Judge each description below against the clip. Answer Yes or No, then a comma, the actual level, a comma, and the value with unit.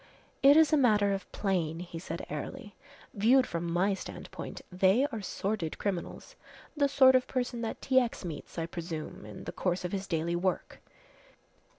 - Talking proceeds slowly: No, average, 175 wpm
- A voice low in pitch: No, high, 195 Hz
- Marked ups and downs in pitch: Yes, wide, 6.2 semitones